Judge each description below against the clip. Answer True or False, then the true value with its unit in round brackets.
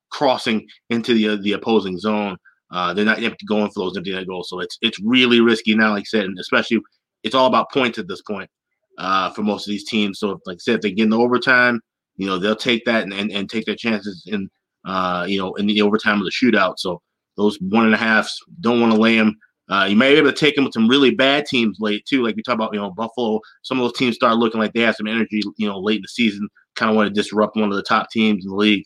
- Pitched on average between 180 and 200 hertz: False (110 Hz)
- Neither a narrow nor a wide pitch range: False (2.1 semitones)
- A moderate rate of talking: False (275 wpm)